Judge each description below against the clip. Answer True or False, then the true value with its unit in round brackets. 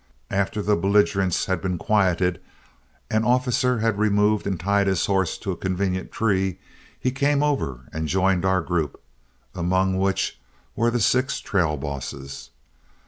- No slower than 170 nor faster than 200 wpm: False (145 wpm)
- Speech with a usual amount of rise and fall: True (3.0 semitones)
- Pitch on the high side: False (95 Hz)